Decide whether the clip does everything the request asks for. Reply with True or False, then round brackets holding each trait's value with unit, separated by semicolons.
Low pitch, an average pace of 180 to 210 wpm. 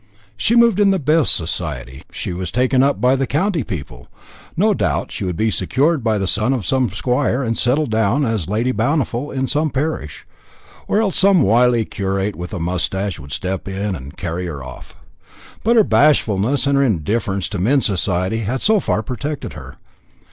True (115 Hz; 190 wpm)